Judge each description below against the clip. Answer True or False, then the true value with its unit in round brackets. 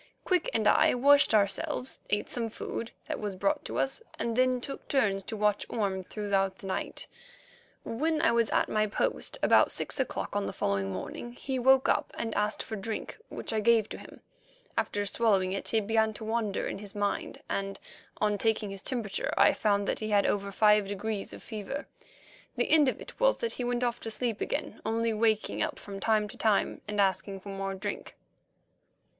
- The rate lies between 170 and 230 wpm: True (200 wpm)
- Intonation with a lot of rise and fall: False (2.7 semitones)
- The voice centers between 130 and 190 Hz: False (215 Hz)